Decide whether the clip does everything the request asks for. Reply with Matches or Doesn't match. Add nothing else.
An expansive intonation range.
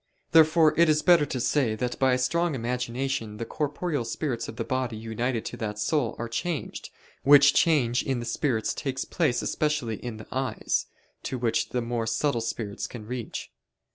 Doesn't match